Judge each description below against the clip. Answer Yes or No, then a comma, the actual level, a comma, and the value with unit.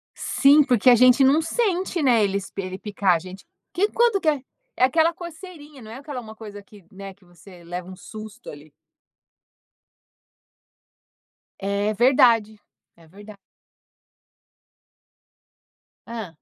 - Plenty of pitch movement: Yes, wide, 6.5 semitones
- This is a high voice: Yes, high, 220 Hz